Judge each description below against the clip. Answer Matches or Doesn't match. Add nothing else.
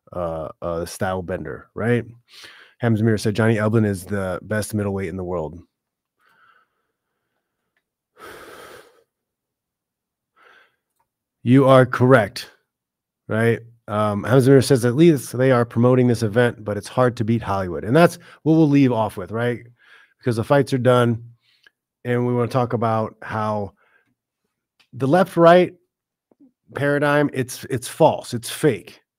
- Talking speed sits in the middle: Doesn't match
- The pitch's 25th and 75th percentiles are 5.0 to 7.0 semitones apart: Doesn't match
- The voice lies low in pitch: Matches